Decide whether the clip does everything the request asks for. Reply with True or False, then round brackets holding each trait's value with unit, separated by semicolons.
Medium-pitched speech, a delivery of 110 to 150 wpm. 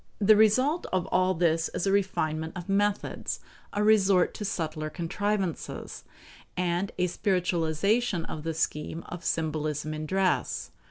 True (180 Hz; 140 wpm)